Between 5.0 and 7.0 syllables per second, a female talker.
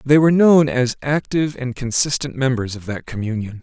No: 5.5 syllables/s; male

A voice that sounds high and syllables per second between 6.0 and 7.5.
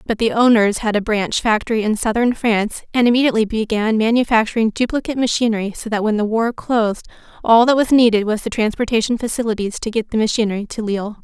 Yes: high, 220 Hz; 6.5 syllables/s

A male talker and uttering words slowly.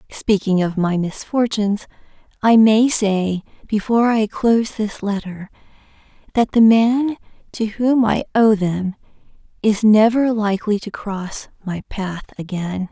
No: female; slow, 130 wpm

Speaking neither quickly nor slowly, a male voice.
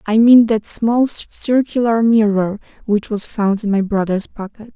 No: average, 165 wpm; female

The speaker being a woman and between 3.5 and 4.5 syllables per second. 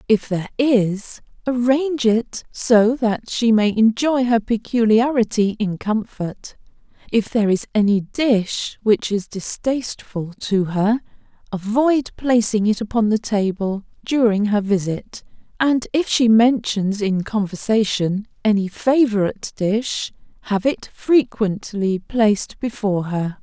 Yes: female; 4.0 syllables/s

